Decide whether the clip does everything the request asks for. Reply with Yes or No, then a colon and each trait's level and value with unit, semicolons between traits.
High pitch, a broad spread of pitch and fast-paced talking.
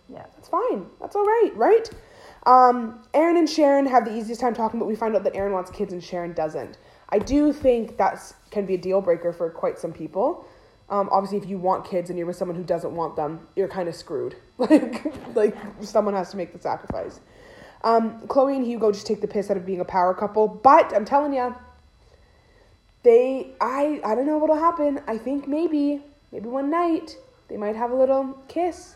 Yes: high, 230 Hz; wide, 6.7 semitones; fast, 215 wpm